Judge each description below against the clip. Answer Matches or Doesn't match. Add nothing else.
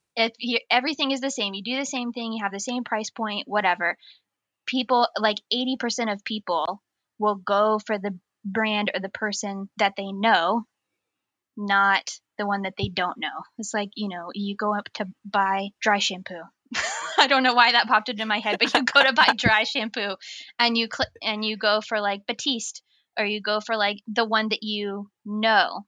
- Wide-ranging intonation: Doesn't match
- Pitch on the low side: Doesn't match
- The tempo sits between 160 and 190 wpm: Doesn't match